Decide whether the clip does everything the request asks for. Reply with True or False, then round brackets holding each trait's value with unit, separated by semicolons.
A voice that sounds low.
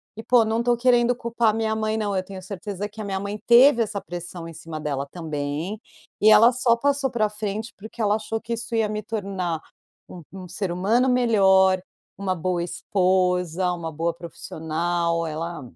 False (200 Hz)